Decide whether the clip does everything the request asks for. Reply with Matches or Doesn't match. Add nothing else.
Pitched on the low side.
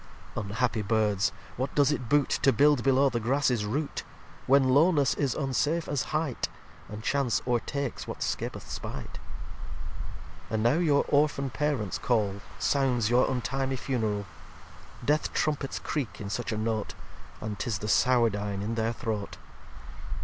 Matches